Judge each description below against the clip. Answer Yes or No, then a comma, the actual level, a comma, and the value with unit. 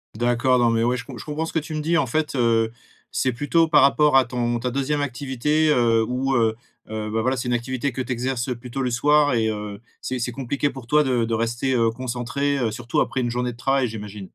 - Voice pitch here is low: Yes, low, 125 Hz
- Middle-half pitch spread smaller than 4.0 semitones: Yes, average, 2.8 semitones